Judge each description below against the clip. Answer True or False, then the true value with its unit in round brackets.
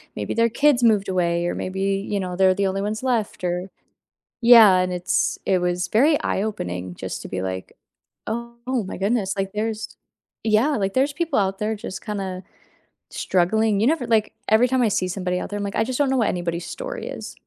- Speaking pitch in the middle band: False (205 Hz)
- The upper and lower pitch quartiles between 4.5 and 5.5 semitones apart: False (4.1 semitones)